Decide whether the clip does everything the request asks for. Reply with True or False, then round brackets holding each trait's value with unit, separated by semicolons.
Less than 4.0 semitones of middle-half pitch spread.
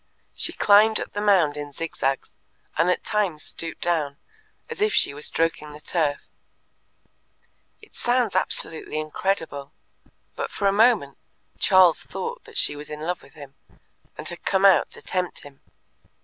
False (5.3 semitones)